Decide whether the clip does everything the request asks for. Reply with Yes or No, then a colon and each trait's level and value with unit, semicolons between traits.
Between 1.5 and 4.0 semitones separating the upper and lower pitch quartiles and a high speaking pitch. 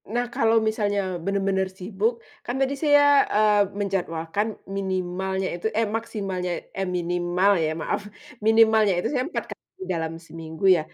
Yes: average, 3.4 semitones; high, 195 Hz